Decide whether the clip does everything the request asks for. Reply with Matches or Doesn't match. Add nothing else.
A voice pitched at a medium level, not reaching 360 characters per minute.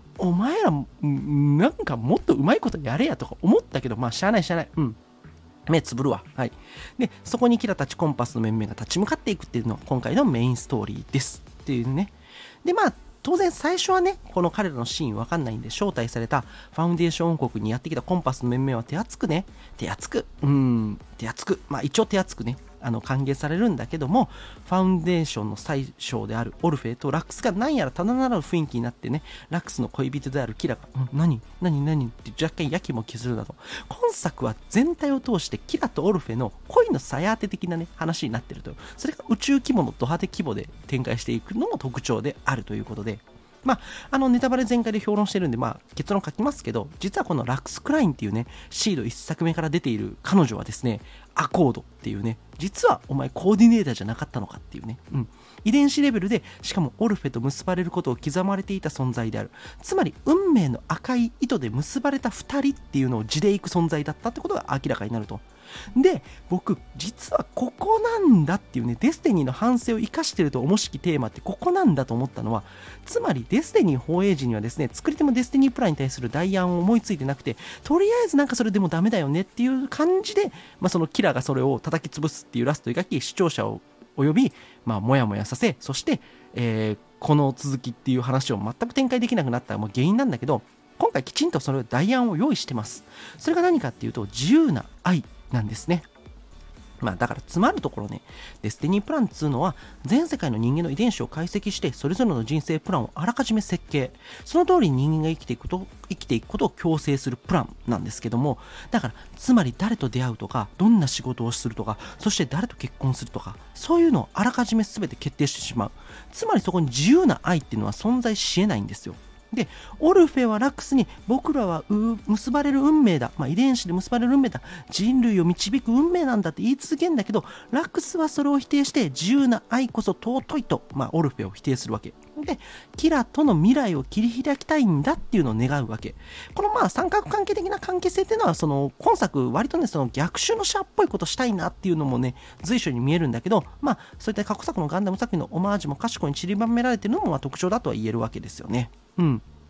Doesn't match